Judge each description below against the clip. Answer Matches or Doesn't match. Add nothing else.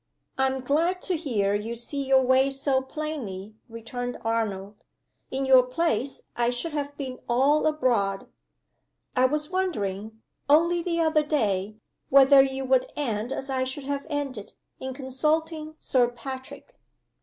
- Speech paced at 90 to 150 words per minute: Matches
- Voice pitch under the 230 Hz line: Doesn't match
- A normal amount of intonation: Matches